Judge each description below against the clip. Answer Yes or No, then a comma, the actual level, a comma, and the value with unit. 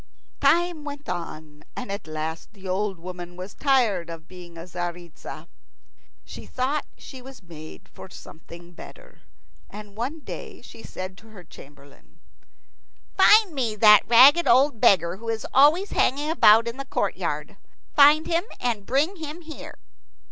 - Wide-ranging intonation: Yes, wide, 8.3 semitones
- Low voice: No, high, 215 Hz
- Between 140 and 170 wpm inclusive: Yes, average, 150 wpm